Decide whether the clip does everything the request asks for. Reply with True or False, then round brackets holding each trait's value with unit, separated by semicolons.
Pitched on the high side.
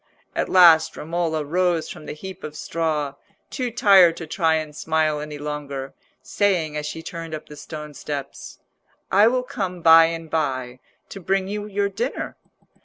False (165 Hz)